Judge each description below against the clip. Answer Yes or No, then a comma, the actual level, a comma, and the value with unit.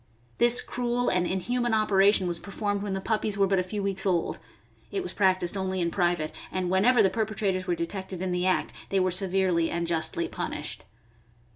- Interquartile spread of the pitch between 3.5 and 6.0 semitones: No, narrow, 2.5 semitones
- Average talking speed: Yes, average, 195 wpm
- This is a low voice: No, high, 190 Hz